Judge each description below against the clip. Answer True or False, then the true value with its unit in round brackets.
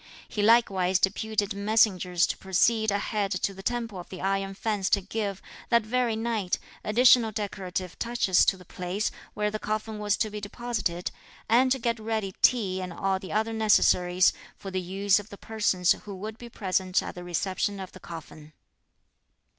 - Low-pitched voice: False (205 Hz)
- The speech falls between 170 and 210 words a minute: True (180 wpm)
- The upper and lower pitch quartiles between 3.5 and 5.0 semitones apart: False (2.8 semitones)